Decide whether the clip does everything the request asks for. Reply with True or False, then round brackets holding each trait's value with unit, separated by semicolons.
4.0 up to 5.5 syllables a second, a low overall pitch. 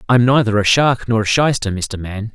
True (5.1 syllables/s; 115 Hz)